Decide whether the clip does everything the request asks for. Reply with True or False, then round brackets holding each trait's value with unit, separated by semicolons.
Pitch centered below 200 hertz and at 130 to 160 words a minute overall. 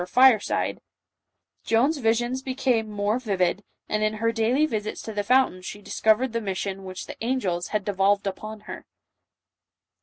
False (215 Hz; 155 wpm)